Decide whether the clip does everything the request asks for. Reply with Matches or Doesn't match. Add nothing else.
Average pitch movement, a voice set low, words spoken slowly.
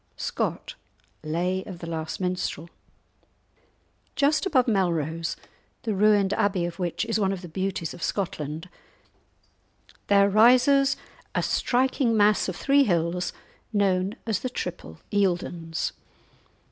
Doesn't match